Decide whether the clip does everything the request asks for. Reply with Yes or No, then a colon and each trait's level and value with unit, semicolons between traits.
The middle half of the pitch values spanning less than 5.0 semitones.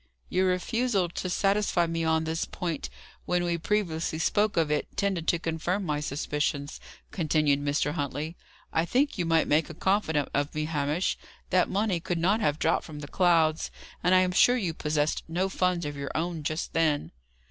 Yes: average, 3.2 semitones